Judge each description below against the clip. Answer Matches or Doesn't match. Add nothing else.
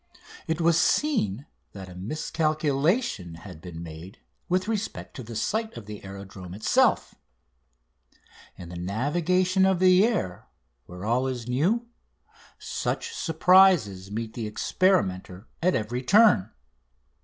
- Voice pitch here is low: Matches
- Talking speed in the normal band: Doesn't match